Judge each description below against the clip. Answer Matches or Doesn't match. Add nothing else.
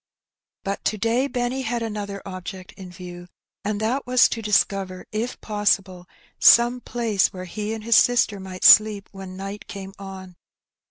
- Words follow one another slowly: Doesn't match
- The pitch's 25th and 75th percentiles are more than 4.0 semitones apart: Doesn't match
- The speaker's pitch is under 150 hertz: Doesn't match